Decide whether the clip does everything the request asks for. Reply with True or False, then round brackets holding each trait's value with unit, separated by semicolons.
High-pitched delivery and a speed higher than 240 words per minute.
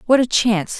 False (225 Hz; 225 wpm)